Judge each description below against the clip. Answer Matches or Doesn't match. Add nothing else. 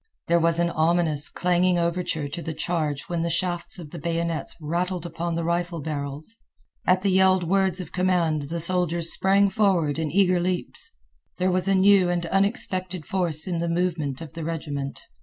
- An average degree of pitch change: Doesn't match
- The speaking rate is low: Doesn't match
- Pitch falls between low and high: Matches